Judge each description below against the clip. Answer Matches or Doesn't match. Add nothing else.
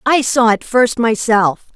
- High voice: Matches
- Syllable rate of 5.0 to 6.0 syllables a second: Doesn't match